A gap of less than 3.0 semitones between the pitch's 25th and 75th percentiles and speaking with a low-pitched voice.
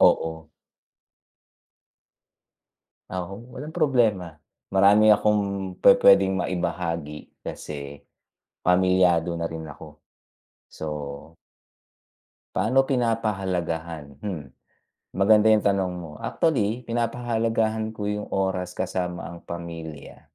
No: average, 4.5 semitones; very low, 95 Hz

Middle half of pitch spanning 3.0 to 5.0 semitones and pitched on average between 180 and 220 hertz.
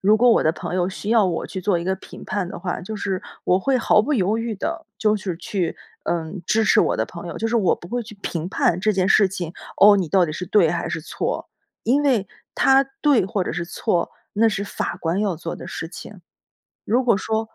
Yes: average, 3.8 semitones; high, 195 Hz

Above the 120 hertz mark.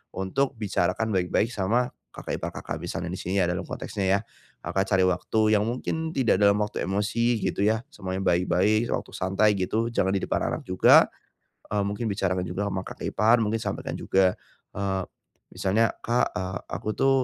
No: low, 100 Hz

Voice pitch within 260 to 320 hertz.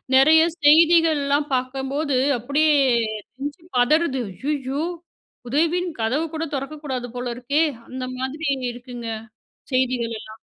Yes: very high, 275 Hz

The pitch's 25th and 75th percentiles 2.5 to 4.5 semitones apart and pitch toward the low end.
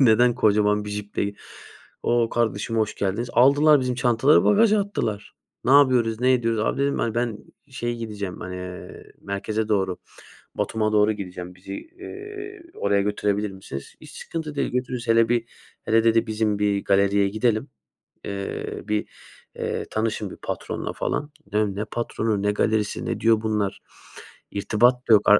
Yes: average, 3.0 semitones; low, 110 Hz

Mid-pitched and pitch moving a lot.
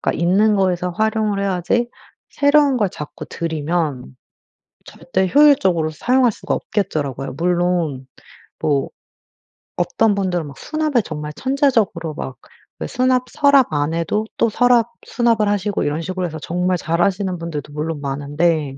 Yes: medium, 180 Hz; wide, 6.1 semitones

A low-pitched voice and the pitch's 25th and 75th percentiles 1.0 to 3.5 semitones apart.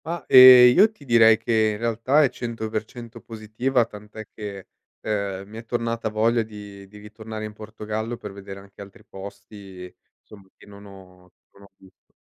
Yes: low, 110 Hz; narrow, 2.5 semitones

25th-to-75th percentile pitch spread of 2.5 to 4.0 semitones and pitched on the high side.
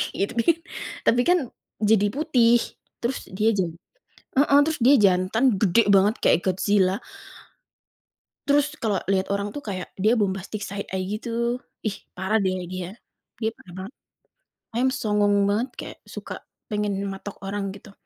Yes: average, 3.5 semitones; high, 205 Hz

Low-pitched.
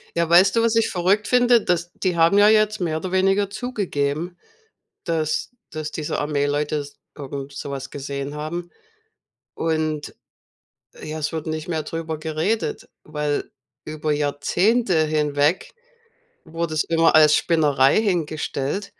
No: medium, 160 Hz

